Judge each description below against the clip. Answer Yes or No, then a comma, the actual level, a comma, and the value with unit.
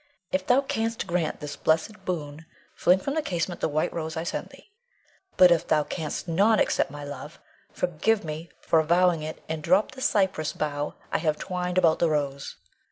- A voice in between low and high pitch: Yes, medium, 165 Hz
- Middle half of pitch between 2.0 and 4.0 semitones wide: Yes, average, 3.3 semitones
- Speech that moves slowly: No, average, 190 wpm